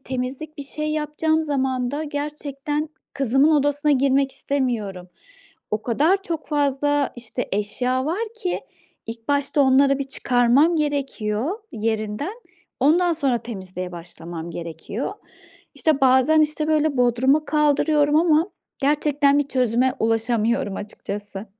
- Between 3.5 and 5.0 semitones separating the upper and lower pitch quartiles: Yes, average, 4.3 semitones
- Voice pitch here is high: Yes, very high, 275 Hz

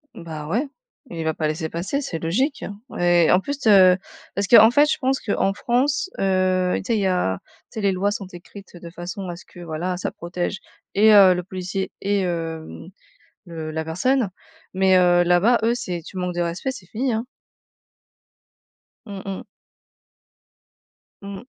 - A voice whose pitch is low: No, medium, 185 Hz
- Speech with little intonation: No, average, 3.0 semitones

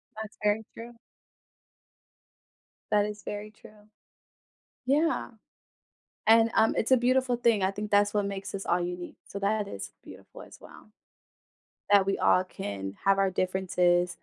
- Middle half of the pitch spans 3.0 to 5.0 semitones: No, narrow, 2.6 semitones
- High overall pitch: Yes, high, 205 Hz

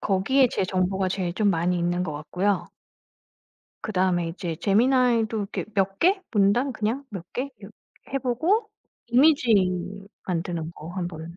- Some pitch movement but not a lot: No, wide, 5.8 semitones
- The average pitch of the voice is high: Yes, high, 195 Hz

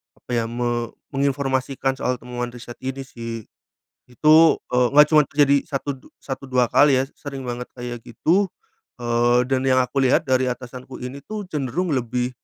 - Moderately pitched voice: No, low, 130 Hz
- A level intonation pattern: Yes, narrow, 2.3 semitones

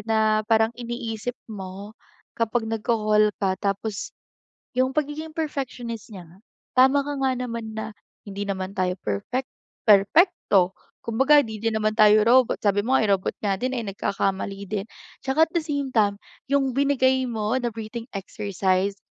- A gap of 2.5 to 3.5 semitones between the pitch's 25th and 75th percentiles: No, average, 4.3 semitones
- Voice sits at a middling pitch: No, high, 220 Hz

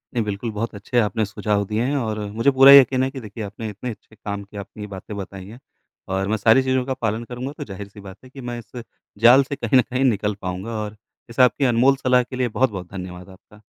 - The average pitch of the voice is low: Yes, low, 110 Hz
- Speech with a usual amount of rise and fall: Yes, average, 3.8 semitones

